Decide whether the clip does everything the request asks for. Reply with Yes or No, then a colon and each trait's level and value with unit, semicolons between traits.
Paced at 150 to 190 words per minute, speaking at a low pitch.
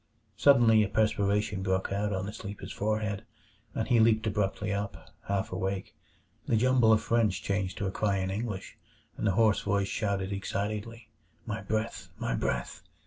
Yes: average, 165 wpm; low, 105 Hz